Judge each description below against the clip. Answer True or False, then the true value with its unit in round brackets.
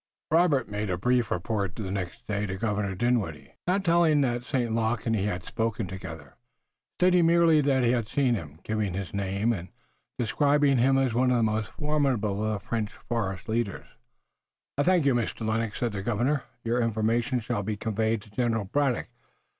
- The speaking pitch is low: True (115 Hz)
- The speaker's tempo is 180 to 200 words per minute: True (185 wpm)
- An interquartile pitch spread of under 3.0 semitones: False (3.9 semitones)